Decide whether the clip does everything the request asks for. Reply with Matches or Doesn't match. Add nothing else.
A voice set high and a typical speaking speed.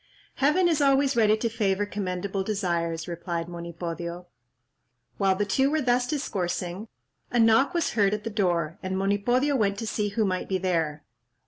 Matches